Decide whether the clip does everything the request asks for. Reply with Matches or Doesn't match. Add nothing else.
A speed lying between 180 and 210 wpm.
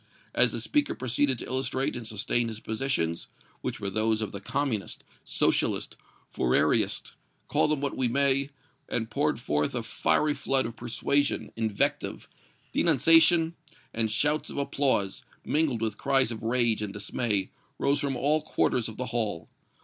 Doesn't match